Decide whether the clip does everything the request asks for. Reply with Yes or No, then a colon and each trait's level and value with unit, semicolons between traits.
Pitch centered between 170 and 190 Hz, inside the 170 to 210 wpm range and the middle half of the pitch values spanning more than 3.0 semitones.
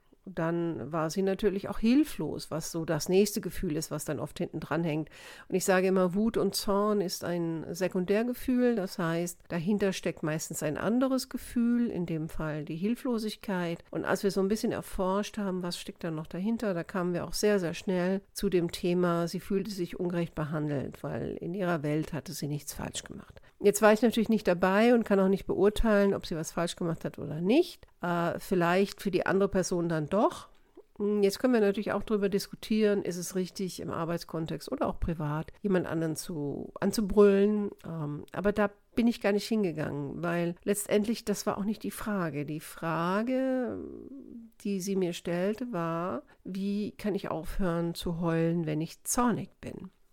Yes: medium, 185 Hz; fast, 190 wpm; average, 3.5 semitones